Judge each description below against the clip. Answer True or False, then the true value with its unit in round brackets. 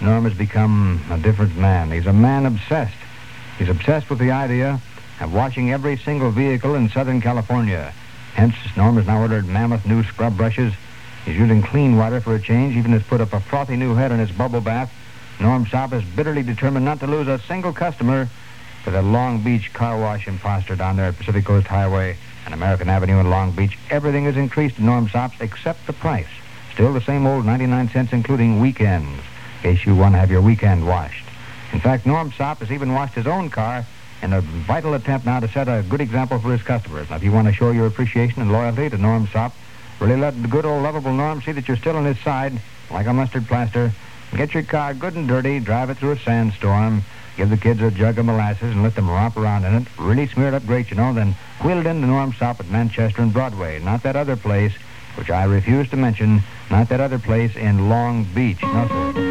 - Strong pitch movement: False (3.6 semitones)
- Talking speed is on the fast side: True (225 wpm)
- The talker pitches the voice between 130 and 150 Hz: False (115 Hz)